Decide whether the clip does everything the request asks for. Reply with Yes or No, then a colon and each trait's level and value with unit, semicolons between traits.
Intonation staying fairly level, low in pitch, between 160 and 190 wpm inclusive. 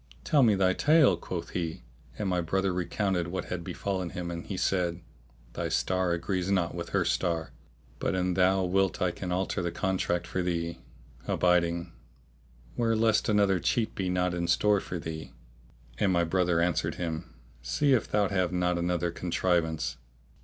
Yes: narrow, 2.0 semitones; very low, 90 Hz; average, 170 wpm